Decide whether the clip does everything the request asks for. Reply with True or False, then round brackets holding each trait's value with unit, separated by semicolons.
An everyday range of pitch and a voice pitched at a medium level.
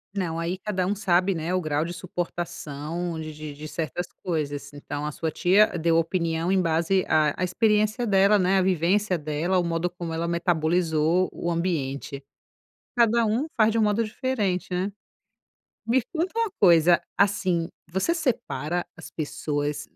True (3.5 semitones; 175 Hz)